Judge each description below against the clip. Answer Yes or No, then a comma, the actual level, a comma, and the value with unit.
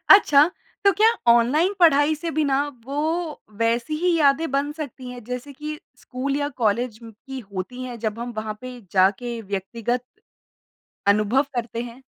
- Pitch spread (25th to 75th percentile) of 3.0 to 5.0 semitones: Yes, average, 3.8 semitones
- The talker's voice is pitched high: Yes, very high, 250 Hz